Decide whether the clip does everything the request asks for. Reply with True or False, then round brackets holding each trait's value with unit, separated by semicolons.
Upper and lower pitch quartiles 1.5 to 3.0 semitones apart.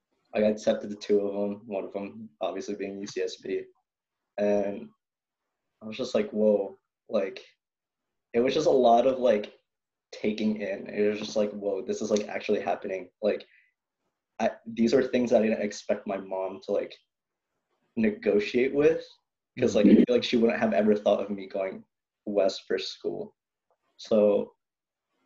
True (2.5 semitones)